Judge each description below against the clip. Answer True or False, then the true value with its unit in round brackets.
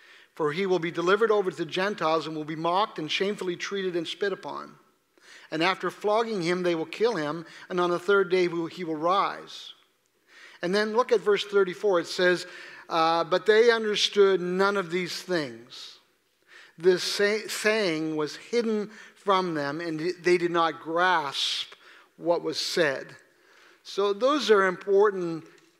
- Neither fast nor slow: True (165 wpm)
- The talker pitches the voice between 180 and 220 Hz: True (185 Hz)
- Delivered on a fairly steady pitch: False (3.3 semitones)